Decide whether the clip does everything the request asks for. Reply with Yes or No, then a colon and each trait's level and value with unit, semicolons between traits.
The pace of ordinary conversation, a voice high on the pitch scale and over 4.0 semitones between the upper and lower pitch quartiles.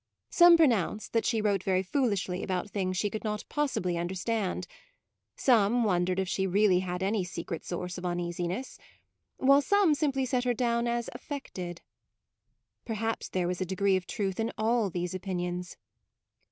Yes: average, 165 wpm; high, 195 Hz; average, 4.7 semitones